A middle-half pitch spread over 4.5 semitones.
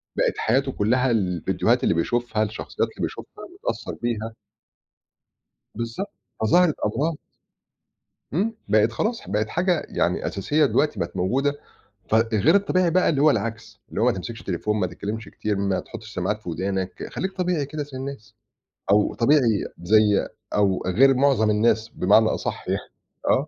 Yes: average, 5.3 semitones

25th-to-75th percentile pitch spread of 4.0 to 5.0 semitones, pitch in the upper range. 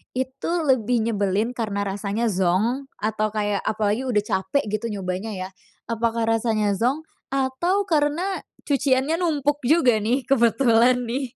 Yes: average, 4.3 semitones; high, 235 Hz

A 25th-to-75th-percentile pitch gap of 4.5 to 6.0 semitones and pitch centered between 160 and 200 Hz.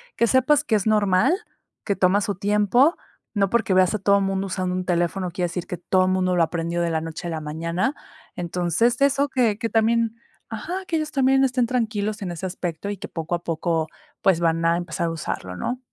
Yes: average, 4.9 semitones; high, 190 Hz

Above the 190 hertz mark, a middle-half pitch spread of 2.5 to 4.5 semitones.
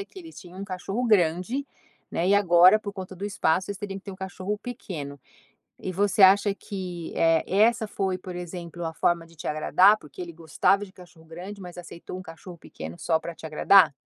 No: medium, 185 Hz; average, 3.0 semitones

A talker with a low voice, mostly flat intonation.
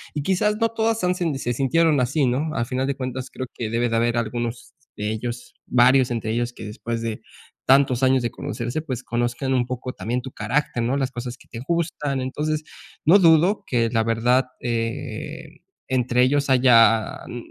No: low, 125 Hz; average, 3.2 semitones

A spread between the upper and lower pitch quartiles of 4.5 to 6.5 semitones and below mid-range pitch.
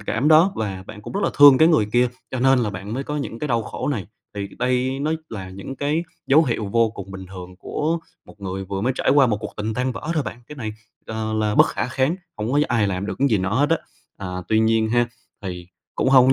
Yes: average, 4.9 semitones; low, 115 Hz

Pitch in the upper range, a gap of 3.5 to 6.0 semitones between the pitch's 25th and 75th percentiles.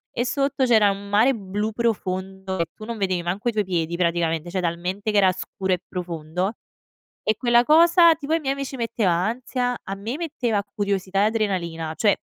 Yes: high, 200 Hz; average, 4.5 semitones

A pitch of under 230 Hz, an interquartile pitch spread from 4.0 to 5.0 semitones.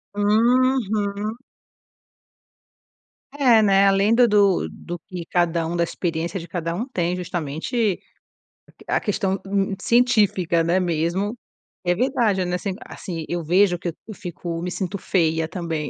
No: medium, 185 Hz; average, 3.5 semitones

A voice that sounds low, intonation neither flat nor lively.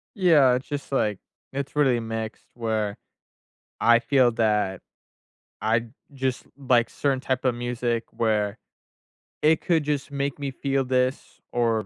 Yes: low, 125 Hz; average, 3.4 semitones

